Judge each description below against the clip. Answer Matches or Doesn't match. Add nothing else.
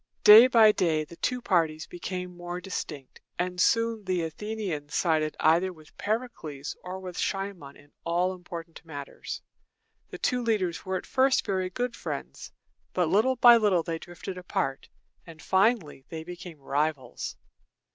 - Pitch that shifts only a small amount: Doesn't match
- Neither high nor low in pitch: Matches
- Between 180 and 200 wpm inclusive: Doesn't match